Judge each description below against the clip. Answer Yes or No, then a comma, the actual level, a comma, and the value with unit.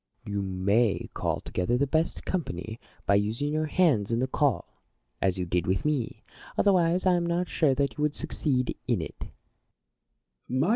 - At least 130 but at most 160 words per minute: No, average, 175 wpm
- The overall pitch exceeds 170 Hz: No, low, 130 Hz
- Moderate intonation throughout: No, wide, 7.5 semitones